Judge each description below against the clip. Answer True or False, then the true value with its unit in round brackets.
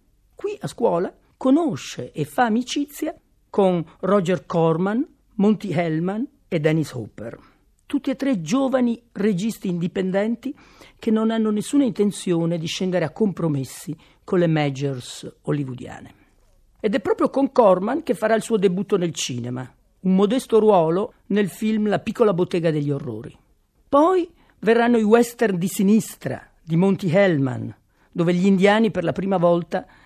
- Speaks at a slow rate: False (140 wpm)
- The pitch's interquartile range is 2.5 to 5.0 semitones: False (5.5 semitones)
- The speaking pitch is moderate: False (195 Hz)